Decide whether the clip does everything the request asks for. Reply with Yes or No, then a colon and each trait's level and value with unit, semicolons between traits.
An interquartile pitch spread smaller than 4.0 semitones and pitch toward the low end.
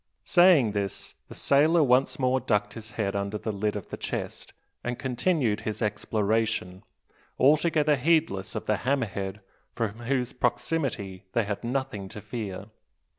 No: average, 4.6 semitones; low, 115 Hz